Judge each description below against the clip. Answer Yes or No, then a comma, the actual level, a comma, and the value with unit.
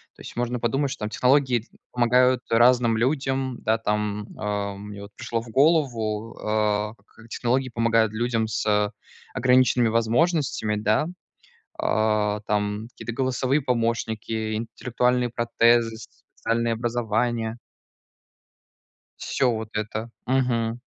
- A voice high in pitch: No, low, 115 Hz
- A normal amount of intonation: No, narrow, 2.3 semitones